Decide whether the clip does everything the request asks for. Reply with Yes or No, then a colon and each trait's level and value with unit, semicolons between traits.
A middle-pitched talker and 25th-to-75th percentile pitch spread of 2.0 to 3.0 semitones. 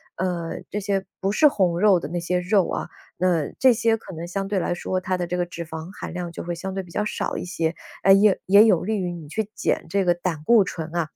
Yes: medium, 180 Hz; narrow, 2.6 semitones